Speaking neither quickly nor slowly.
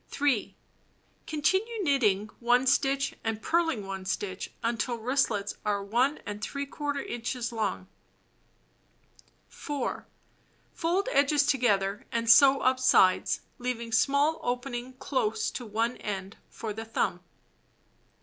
No: slow, 110 wpm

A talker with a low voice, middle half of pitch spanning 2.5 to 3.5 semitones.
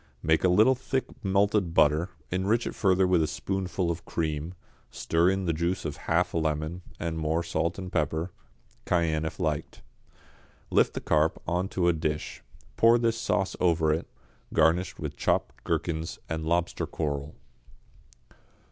Yes: very low, 85 Hz; average, 2.9 semitones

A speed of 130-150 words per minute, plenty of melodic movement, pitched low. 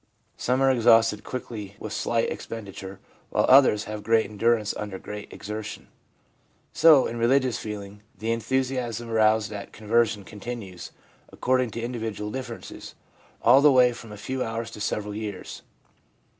No: average, 145 wpm; narrow, 2.6 semitones; low, 115 Hz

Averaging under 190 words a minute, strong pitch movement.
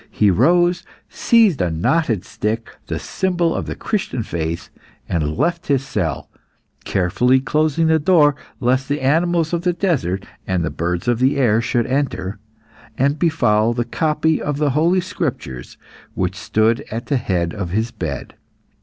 Yes: average, 160 wpm; wide, 8.3 semitones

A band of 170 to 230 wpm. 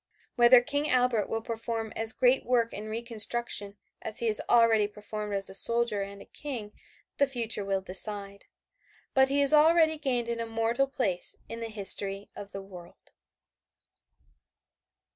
No: average, 155 wpm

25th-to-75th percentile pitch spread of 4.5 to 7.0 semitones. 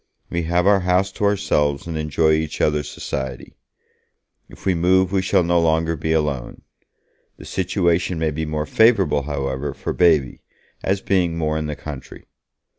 No: average, 3.3 semitones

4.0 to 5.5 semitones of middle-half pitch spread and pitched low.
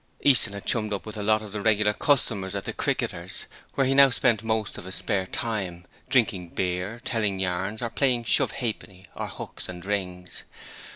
No: average, 3.3 semitones; low, 105 Hz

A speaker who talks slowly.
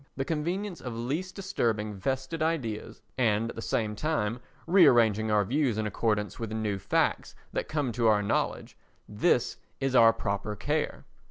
No: average, 160 wpm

